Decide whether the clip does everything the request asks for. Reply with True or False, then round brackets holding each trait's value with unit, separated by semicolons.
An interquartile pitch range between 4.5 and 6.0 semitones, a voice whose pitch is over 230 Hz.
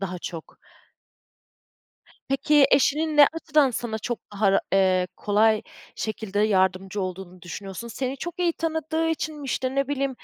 False (7.2 semitones; 240 Hz)